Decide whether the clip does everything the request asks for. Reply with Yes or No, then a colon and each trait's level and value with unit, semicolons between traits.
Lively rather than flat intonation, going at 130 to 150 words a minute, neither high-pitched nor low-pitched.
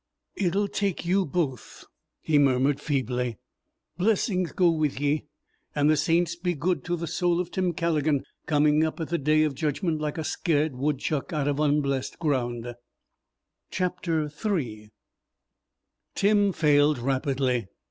No: average, 3.8 semitones; slow, 135 wpm; medium, 150 Hz